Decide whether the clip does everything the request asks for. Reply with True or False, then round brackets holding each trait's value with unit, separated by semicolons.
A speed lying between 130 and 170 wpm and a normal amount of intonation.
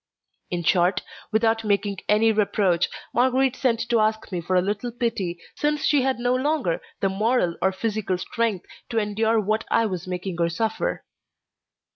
True (165 wpm; 3.7 semitones)